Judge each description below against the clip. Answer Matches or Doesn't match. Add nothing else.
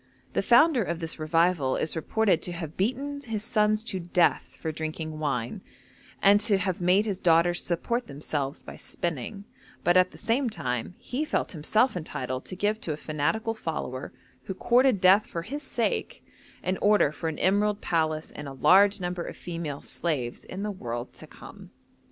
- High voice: Doesn't match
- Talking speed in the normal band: Matches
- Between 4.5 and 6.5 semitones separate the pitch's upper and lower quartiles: Matches